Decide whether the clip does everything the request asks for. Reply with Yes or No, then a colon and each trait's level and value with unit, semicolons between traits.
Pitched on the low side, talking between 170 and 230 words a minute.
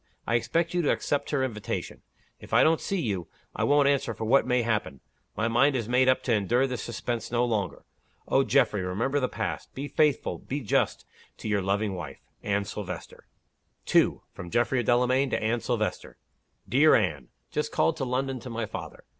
Yes: low, 120 Hz; average, 190 wpm